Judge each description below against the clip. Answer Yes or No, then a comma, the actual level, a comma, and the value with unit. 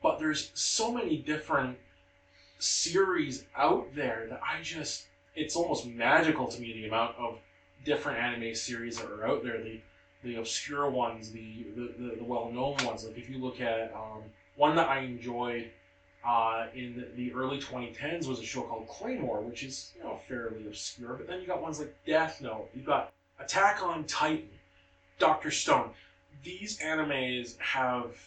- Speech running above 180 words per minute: No, average, 170 wpm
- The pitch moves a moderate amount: Yes, average, 4.0 semitones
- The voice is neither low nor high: No, low, 120 Hz